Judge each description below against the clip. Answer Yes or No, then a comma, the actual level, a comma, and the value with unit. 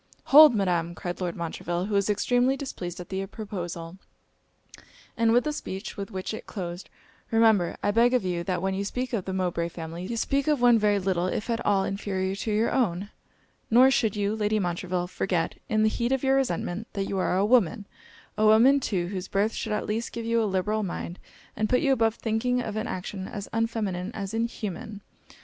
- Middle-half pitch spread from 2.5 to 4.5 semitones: Yes, average, 3.7 semitones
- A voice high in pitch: Yes, high, 205 Hz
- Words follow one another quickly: Yes, fast, 210 wpm